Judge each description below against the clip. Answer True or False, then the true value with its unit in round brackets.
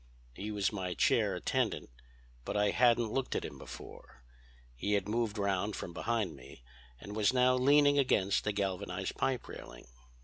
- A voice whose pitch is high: False (105 Hz)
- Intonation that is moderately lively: True (3.9 semitones)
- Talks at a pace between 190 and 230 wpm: False (165 wpm)